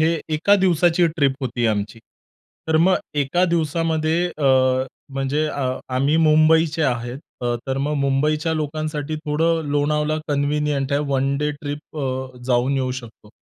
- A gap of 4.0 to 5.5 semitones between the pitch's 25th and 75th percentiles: No, average, 2.7 semitones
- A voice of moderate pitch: Yes, medium, 150 Hz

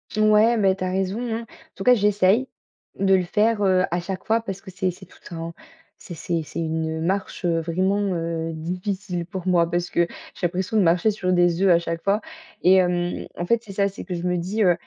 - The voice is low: No, medium, 185 Hz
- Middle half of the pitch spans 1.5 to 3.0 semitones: Yes, narrow, 2.5 semitones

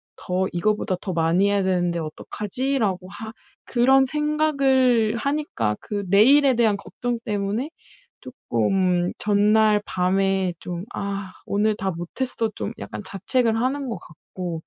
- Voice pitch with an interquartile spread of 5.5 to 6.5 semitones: No, average, 5.1 semitones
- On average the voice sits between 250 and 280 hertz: No, high, 205 Hz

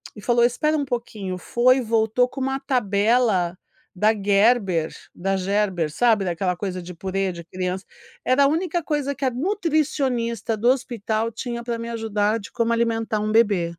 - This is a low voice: No, high, 225 Hz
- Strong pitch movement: No, average, 4.3 semitones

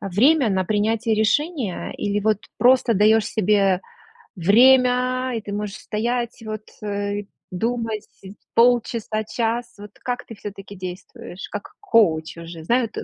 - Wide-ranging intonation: No, average, 2.9 semitones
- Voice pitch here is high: Yes, high, 215 Hz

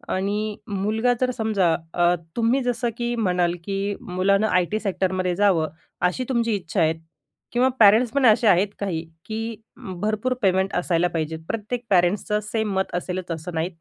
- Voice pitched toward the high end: Yes, high, 200 Hz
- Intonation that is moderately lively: Yes, average, 3.9 semitones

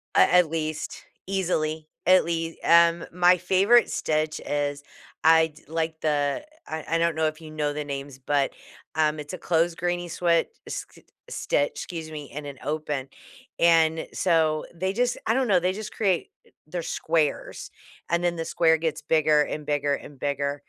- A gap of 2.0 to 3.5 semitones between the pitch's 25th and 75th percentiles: Yes, narrow, 2.5 semitones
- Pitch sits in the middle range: Yes, medium, 160 Hz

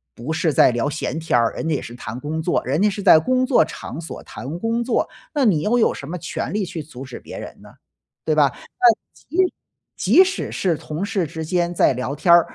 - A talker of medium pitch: Yes, medium, 165 Hz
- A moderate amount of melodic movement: No, wide, 6.1 semitones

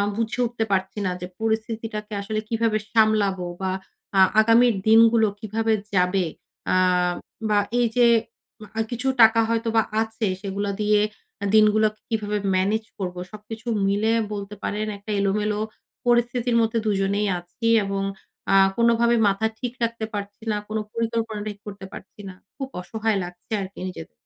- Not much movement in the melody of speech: Yes, narrow, 2.1 semitones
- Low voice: No, high, 215 Hz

